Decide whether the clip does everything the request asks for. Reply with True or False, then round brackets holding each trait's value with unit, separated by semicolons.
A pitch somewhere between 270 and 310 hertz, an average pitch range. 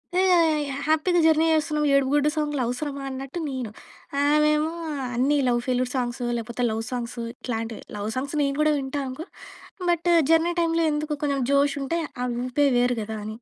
True (280 Hz; 3.5 semitones)